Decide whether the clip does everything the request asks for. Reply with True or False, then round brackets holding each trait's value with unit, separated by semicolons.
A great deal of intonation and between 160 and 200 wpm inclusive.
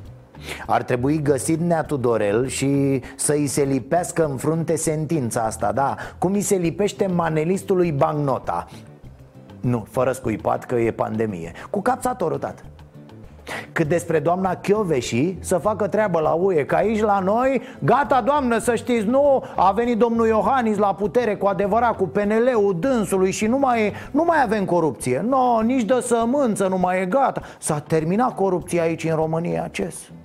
True (7.8 semitones; 165 wpm)